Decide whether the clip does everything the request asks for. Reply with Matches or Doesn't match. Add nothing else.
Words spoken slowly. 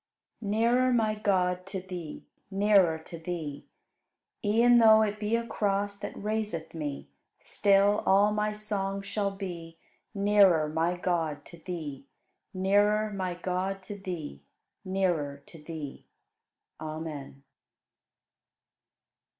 Matches